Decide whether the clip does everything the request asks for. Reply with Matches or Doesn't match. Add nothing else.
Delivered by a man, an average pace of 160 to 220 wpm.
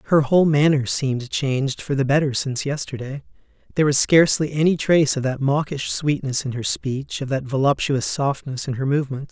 Matches